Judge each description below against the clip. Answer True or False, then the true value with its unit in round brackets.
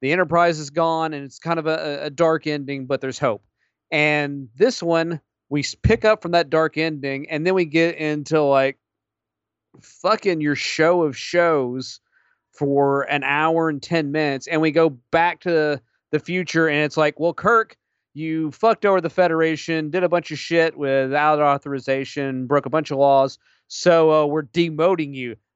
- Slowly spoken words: False (180 wpm)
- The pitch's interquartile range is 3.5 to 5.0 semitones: False (3.0 semitones)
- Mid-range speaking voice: True (155 Hz)